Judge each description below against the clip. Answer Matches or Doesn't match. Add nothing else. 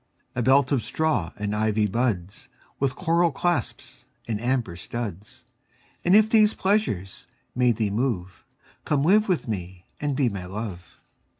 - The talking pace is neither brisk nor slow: Matches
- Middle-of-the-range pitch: Doesn't match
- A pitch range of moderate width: Doesn't match